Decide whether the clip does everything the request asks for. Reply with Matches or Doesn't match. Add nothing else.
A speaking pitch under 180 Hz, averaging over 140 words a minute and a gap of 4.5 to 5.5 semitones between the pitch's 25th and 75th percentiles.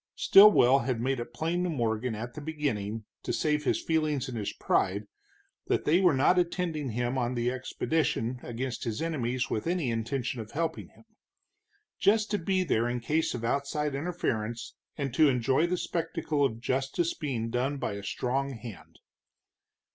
Matches